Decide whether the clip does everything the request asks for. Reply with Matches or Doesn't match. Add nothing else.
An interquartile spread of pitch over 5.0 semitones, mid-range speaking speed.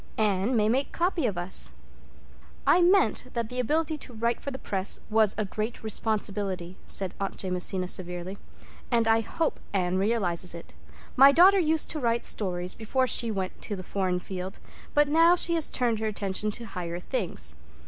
Matches